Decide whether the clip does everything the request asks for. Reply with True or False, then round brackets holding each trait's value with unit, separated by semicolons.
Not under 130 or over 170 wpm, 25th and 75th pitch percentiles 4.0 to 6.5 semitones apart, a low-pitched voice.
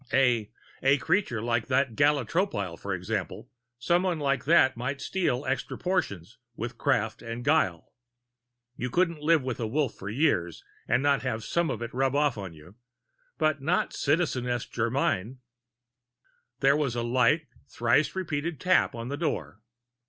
True (155 wpm; 4.6 semitones; 130 Hz)